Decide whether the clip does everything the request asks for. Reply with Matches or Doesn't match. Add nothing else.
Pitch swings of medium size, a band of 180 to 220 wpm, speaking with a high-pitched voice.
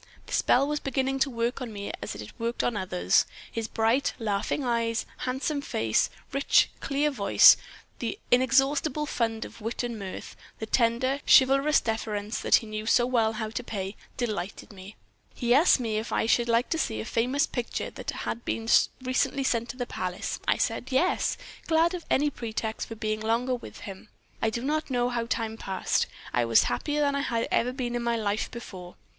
Matches